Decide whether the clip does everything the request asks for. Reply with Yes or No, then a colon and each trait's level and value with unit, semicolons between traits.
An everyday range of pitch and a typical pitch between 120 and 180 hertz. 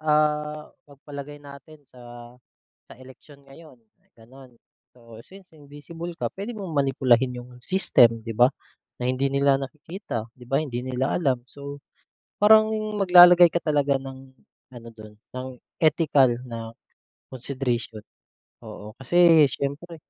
Yes: average, 3.8 semitones; medium, 140 Hz